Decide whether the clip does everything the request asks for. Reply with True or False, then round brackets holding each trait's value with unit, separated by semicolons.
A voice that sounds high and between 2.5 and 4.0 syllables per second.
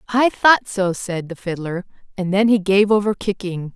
False (195 Hz; 4.6 syllables/s)